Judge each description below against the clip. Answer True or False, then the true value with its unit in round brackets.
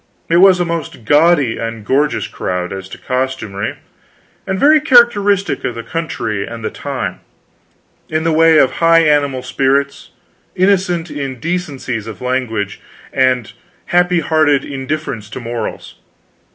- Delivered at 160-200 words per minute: False (135 wpm)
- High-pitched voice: False (140 Hz)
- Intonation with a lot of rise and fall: True (6.1 semitones)